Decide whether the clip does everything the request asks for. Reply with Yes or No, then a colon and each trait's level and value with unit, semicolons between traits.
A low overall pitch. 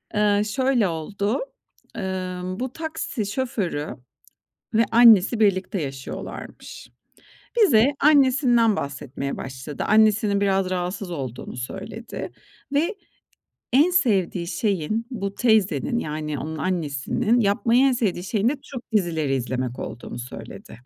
No: high, 200 Hz